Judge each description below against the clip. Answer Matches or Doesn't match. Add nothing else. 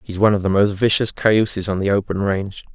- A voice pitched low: Matches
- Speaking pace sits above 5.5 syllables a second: Matches